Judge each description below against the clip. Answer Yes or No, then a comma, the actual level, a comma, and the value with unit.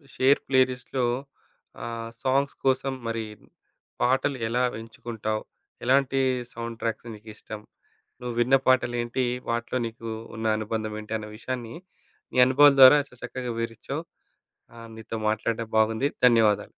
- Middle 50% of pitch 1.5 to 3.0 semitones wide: Yes, narrow, 2.4 semitones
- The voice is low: Yes, low, 120 Hz